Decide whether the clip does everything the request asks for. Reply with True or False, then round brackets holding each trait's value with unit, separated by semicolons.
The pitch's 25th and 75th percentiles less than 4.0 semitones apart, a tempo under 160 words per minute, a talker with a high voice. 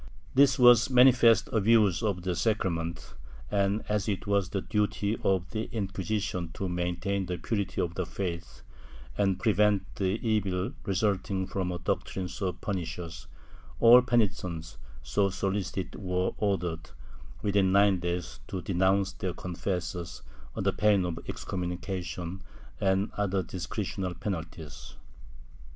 False (2.5 semitones; 135 wpm; 95 Hz)